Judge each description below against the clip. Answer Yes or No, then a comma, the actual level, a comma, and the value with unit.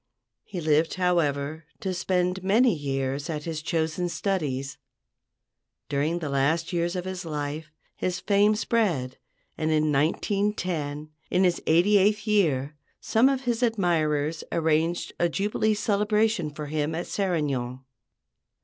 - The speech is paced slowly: Yes, slow, 130 wpm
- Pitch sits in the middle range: Yes, medium, 170 Hz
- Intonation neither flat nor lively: Yes, average, 4.5 semitones